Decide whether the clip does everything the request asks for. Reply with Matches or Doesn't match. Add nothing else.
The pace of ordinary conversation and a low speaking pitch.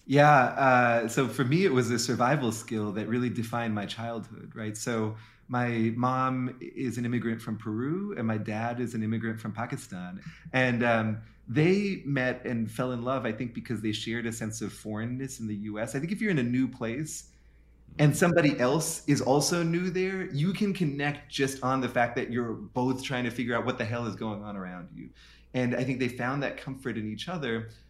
Doesn't match